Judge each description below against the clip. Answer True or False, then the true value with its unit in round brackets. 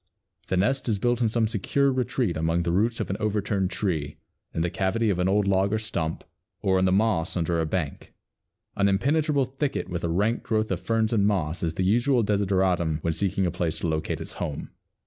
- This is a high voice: False (100 Hz)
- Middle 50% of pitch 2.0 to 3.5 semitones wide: False (4.4 semitones)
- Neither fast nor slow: False (215 wpm)